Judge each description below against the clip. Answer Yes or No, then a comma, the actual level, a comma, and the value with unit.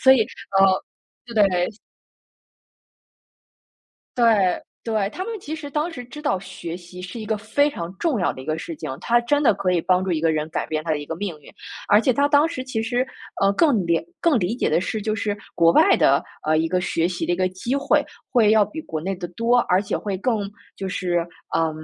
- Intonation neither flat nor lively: No, wide, 6.0 semitones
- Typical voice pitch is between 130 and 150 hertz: No, high, 200 Hz